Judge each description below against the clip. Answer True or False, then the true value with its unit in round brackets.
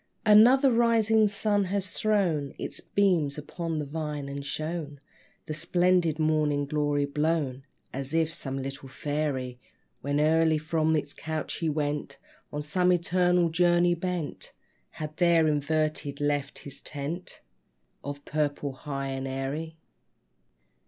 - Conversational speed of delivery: False (130 wpm)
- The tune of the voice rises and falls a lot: False (3.3 semitones)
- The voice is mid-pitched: True (155 Hz)